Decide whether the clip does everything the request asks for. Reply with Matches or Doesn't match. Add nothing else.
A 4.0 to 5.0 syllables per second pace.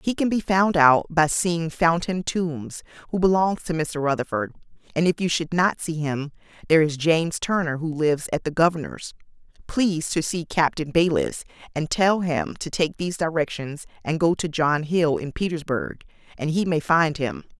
Matches